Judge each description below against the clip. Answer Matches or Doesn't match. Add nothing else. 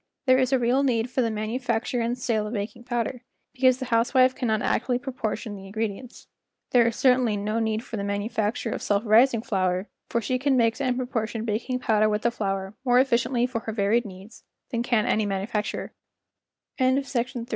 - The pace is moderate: Matches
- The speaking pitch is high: Matches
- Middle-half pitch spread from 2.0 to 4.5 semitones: Matches